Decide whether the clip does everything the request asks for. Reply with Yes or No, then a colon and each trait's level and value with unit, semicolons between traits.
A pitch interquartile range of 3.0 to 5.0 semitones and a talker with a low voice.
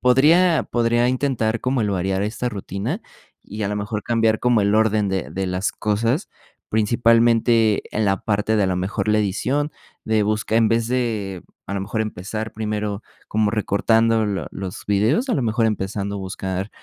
No: narrow, 2.5 semitones; low, 110 Hz